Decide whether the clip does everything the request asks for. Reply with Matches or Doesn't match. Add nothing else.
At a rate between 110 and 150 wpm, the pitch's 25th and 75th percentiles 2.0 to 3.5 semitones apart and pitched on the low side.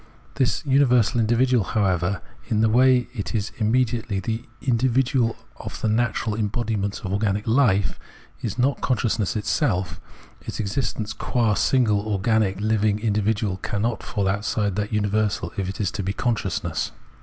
Matches